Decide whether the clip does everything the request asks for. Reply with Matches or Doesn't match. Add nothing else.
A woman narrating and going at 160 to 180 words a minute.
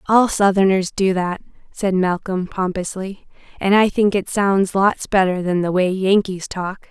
Matches